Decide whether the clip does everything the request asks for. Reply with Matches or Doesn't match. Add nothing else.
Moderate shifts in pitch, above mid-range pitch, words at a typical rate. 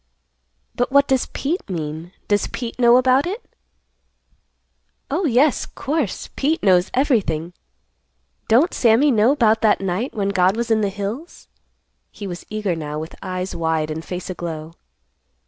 Doesn't match